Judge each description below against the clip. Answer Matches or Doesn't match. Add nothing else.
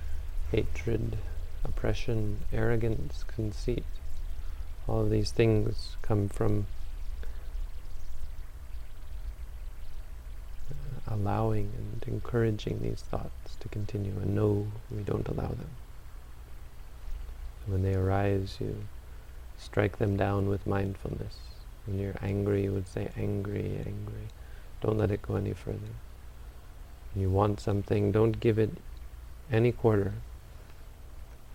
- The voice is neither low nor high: Doesn't match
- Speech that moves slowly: Matches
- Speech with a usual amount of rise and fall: Doesn't match